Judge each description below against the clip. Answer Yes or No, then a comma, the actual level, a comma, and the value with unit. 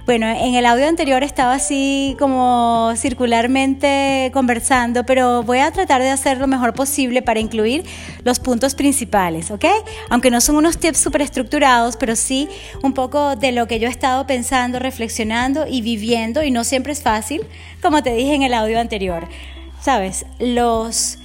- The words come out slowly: No, average, 165 wpm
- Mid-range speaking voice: No, very high, 255 Hz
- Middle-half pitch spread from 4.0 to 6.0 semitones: No, average, 2.9 semitones